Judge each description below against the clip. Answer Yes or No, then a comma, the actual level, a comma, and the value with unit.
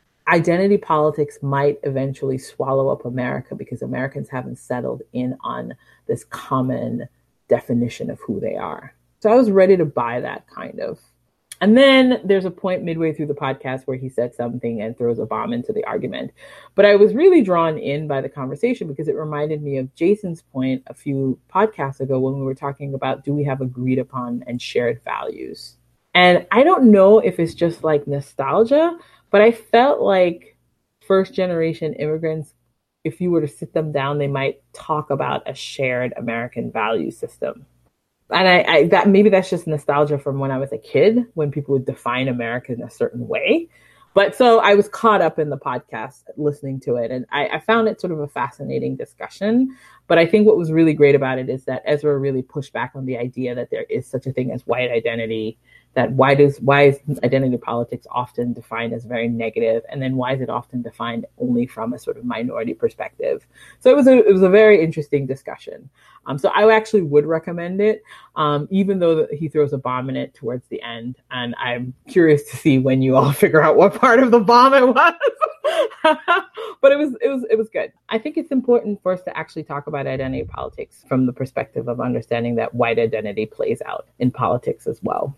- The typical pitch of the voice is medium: Yes, medium, 145 Hz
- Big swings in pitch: Yes, wide, 7.3 semitones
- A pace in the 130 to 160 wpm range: No, fast, 205 wpm